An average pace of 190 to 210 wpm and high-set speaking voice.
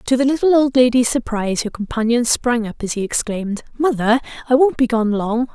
Yes: fast, 205 wpm; high, 240 Hz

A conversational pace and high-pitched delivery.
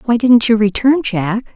Yes: average, 195 wpm; high, 225 Hz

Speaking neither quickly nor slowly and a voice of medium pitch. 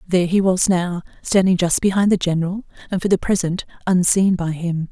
Yes: average, 195 wpm; medium, 180 Hz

